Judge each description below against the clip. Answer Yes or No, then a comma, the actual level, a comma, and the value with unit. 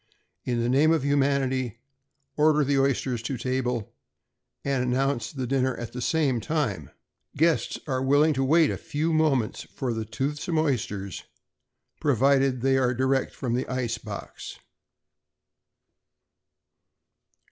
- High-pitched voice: No, low, 130 Hz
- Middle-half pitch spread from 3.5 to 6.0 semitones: No, average, 2.7 semitones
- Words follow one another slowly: Yes, slow, 125 wpm